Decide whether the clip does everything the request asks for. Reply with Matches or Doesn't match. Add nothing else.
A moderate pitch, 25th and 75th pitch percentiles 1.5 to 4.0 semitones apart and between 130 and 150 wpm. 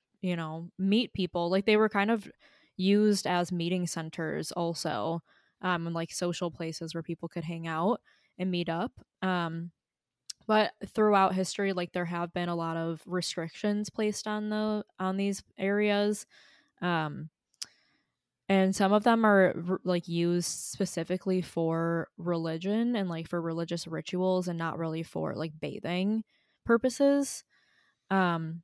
Matches